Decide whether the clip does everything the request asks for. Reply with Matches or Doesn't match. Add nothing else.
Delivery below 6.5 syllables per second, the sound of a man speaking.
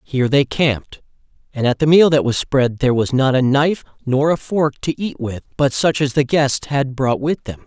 Matches